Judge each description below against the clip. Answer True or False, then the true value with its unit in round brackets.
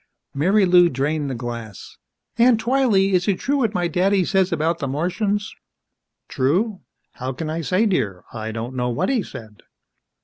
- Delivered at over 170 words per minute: False (165 wpm)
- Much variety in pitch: True (7.5 semitones)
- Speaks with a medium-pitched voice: True (175 Hz)